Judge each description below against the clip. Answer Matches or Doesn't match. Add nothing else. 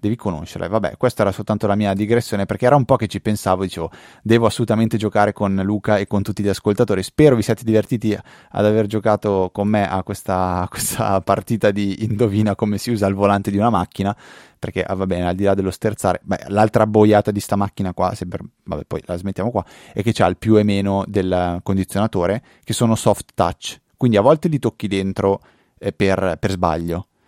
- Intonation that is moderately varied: Doesn't match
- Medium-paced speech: Doesn't match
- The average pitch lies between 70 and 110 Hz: Matches